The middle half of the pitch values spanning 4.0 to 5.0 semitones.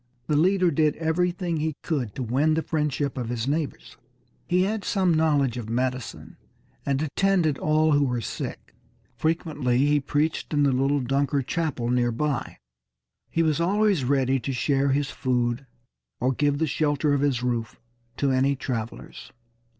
No: average, 3.5 semitones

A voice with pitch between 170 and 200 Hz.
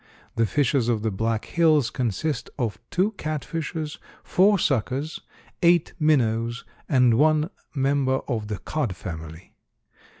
No: low, 135 Hz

